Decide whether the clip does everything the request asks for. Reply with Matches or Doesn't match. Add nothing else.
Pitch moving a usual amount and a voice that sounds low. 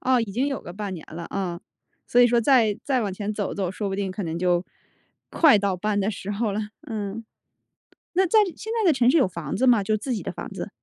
Doesn't match